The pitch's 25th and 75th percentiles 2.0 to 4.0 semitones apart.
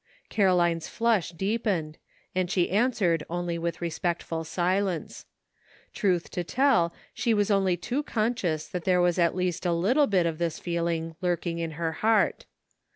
Yes: average, 3.1 semitones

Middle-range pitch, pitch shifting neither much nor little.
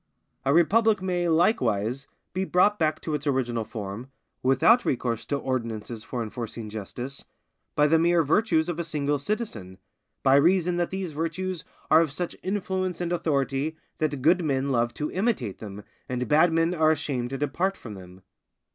No: medium, 150 Hz; wide, 5.9 semitones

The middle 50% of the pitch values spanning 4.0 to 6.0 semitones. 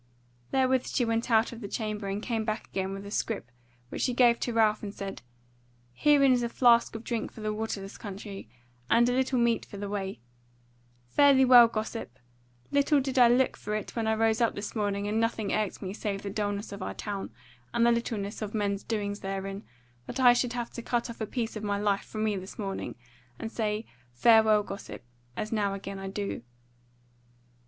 No: average, 2.7 semitones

